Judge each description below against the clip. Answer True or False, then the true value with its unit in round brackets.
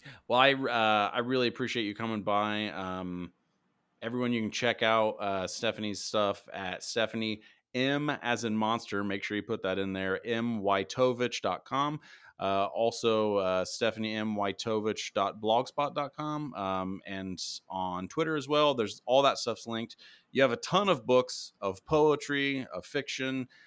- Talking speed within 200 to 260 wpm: False (145 wpm)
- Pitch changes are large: False (4.4 semitones)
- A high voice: False (110 Hz)